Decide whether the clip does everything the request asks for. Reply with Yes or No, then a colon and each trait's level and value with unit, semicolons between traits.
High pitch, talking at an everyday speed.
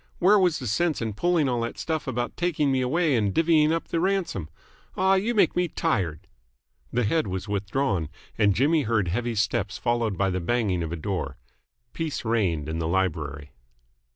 No: low, 120 Hz; average, 185 wpm